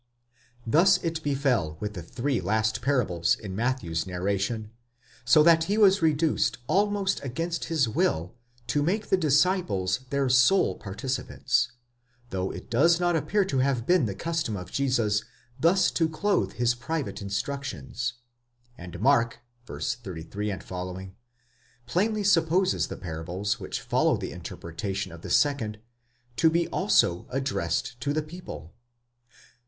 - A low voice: Yes, low, 130 Hz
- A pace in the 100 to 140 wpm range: Yes, slow, 135 wpm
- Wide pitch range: Yes, wide, 8.3 semitones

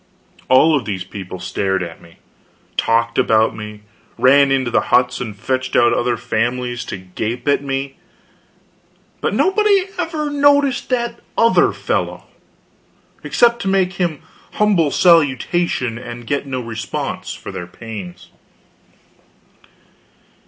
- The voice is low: Yes, low, 130 Hz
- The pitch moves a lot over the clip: Yes, wide, 8.1 semitones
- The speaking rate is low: Yes, slow, 125 wpm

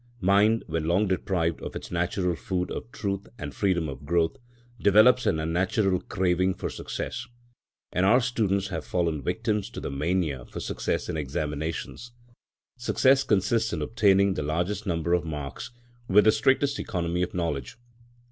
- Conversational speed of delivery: Yes, average, 155 wpm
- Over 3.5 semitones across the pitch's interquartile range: Yes, average, 4.0 semitones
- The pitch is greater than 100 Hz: No, very low, 90 Hz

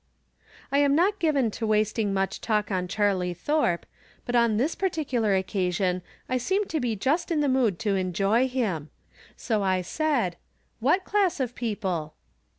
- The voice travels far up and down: Yes, wide, 6.6 semitones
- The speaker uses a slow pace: No, average, 165 wpm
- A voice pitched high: Yes, high, 225 Hz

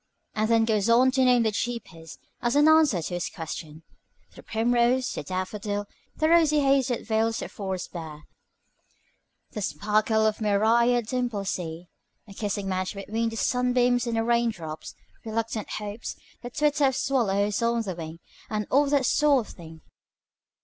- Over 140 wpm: Yes, average, 170 wpm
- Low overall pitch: No, high, 225 Hz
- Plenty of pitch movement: No, average, 3.8 semitones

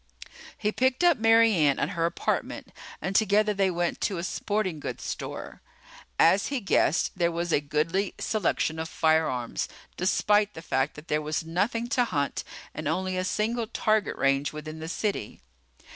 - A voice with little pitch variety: No, average, 5.1 semitones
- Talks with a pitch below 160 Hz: No, medium, 180 Hz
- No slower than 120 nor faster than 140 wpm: No, average, 170 wpm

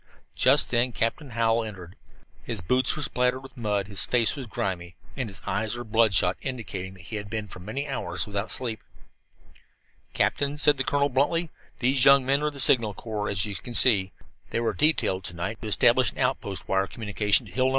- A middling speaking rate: No, fast, 210 wpm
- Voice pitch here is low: Yes, low, 115 Hz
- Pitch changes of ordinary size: Yes, average, 4.5 semitones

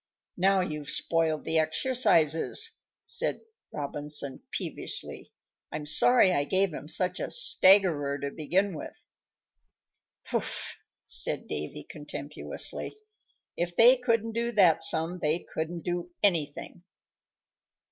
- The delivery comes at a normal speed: No, slow, 110 wpm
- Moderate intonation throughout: Yes, average, 4.4 semitones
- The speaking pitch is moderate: Yes, medium, 165 Hz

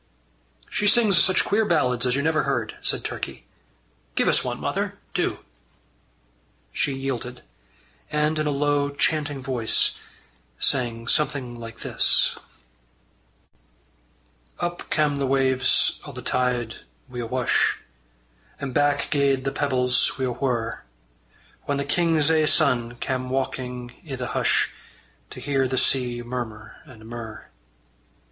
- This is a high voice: No, low, 130 Hz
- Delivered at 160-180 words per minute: No, slow, 135 wpm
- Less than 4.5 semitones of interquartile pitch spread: Yes, average, 2.8 semitones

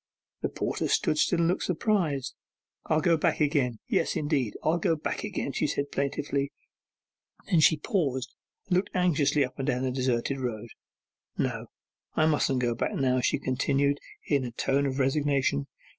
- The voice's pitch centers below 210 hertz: Yes, medium, 140 Hz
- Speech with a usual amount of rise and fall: Yes, average, 3.1 semitones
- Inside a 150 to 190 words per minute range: Yes, average, 170 wpm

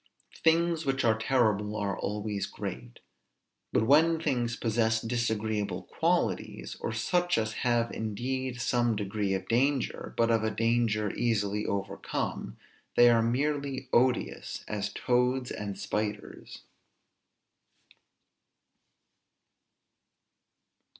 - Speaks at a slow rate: Yes, slow, 105 wpm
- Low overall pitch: Yes, low, 115 Hz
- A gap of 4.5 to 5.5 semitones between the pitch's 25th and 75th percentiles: No, average, 3.2 semitones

